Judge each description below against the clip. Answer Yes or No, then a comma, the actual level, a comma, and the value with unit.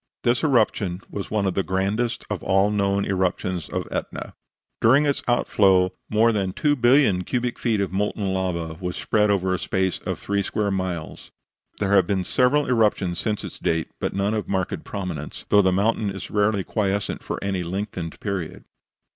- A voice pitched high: No, low, 100 Hz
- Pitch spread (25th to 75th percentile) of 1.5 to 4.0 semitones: Yes, narrow, 2.5 semitones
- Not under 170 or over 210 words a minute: Yes, average, 180 wpm